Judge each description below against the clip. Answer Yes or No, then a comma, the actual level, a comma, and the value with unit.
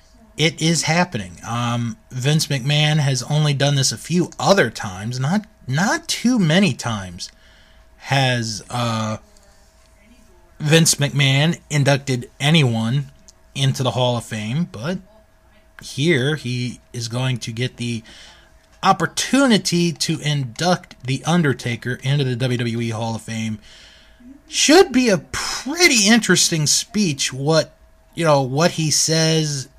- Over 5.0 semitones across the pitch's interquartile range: Yes, wide, 5.5 semitones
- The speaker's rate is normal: No, slow, 125 wpm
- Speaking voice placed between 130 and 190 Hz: Yes, medium, 140 Hz